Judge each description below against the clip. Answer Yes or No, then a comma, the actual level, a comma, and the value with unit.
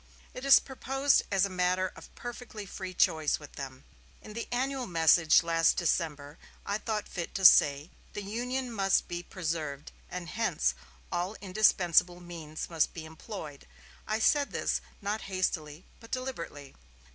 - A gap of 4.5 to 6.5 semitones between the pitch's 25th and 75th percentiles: Yes, average, 5.2 semitones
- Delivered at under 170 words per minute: Yes, average, 150 wpm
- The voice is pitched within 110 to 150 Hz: No, medium, 185 Hz